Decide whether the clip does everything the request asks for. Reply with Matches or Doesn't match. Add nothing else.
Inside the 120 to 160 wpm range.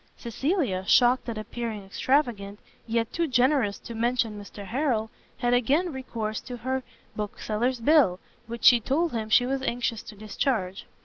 Matches